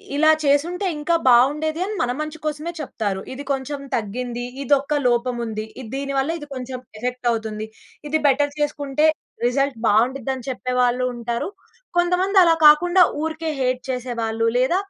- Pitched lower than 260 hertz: No, very high, 270 Hz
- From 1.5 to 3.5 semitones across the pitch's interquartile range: No, average, 3.9 semitones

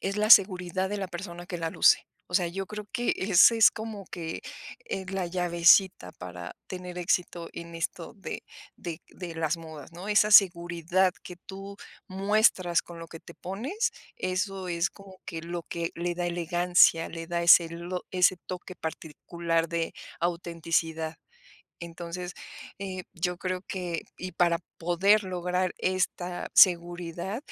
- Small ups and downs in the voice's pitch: Yes, narrow, 2.0 semitones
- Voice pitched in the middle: Yes, medium, 175 Hz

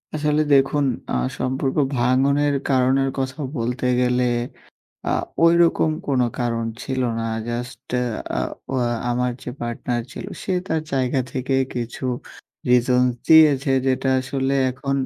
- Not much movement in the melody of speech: Yes, narrow, 1.9 semitones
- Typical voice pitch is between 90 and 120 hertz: No, low, 130 Hz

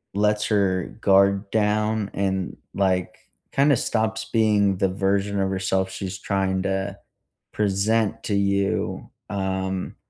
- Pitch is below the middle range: Yes, low, 100 Hz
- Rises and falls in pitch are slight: Yes, narrow, 1.6 semitones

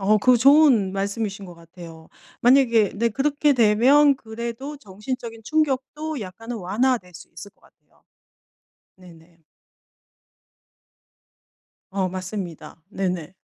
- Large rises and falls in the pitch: Yes, wide, 5.8 semitones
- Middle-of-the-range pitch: No, high, 215 Hz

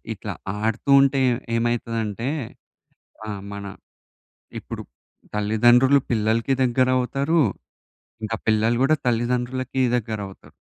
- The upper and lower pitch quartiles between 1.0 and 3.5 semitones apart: Yes, average, 2.8 semitones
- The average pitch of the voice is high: No, low, 120 Hz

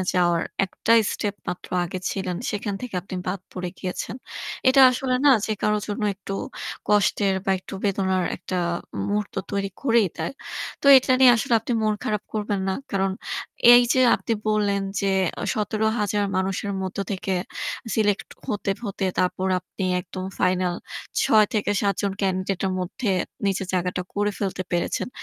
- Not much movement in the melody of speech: Yes, narrow, 2.2 semitones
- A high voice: Yes, high, 200 Hz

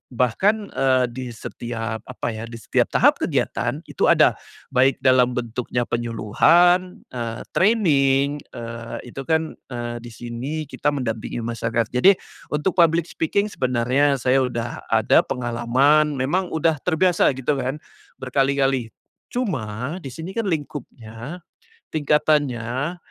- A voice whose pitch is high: No, low, 130 Hz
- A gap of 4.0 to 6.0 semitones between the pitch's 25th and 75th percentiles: Yes, average, 4.6 semitones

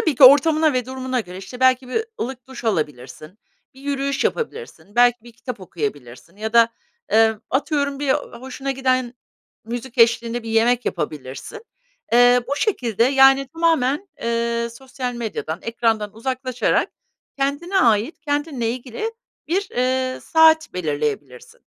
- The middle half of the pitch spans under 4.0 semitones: Yes, average, 3.5 semitones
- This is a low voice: No, very high, 250 Hz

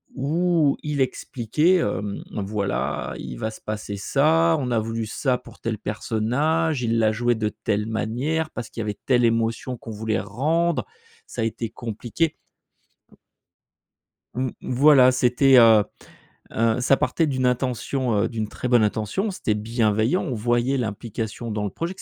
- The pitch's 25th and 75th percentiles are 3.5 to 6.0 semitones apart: Yes, average, 3.9 semitones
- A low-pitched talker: Yes, low, 120 Hz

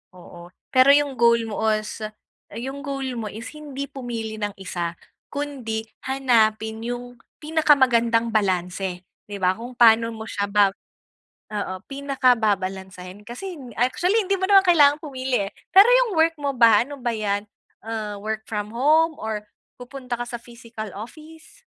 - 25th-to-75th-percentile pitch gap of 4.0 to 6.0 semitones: Yes, average, 4.6 semitones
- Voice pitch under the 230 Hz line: No, high, 235 Hz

